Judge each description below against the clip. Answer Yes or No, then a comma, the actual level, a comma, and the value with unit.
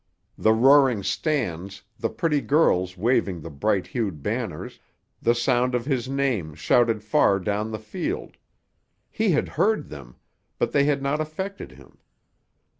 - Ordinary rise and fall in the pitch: No, wide, 6.2 semitones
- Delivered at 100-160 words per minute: Yes, average, 140 wpm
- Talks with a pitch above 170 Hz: No, low, 120 Hz